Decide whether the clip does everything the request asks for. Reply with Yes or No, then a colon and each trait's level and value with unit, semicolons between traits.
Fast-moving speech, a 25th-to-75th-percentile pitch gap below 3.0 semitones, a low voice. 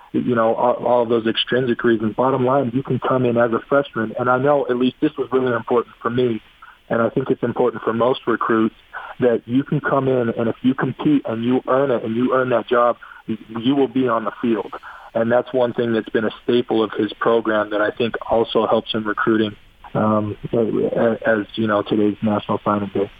Yes: fast, 220 wpm; narrow, 2.5 semitones; low, 120 Hz